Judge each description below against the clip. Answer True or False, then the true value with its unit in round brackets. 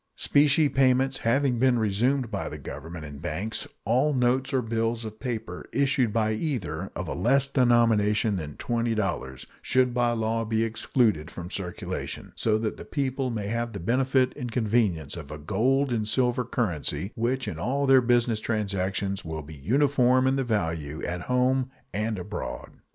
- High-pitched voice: False (115 Hz)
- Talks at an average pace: True (165 wpm)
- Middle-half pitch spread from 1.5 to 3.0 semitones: False (4.6 semitones)